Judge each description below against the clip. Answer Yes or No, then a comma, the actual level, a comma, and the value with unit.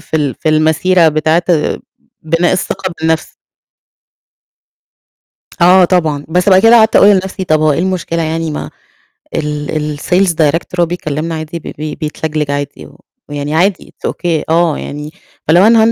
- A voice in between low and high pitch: Yes, medium, 160 Hz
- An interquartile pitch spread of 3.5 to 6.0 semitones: No, average, 2.9 semitones